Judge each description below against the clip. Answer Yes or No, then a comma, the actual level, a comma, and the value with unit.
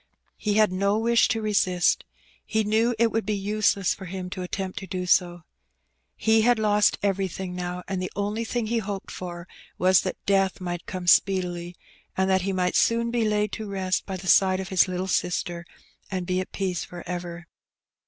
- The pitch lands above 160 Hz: Yes, high, 190 Hz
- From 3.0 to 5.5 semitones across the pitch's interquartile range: No, narrow, 2.6 semitones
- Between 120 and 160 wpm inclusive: No, average, 195 wpm